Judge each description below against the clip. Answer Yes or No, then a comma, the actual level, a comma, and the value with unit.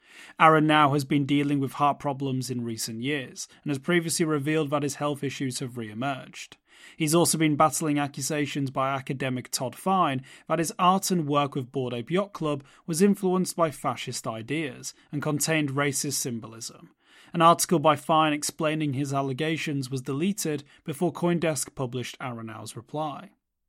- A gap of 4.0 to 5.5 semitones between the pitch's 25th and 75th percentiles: No, average, 2.9 semitones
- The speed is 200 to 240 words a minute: No, average, 160 wpm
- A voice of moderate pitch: Yes, medium, 145 Hz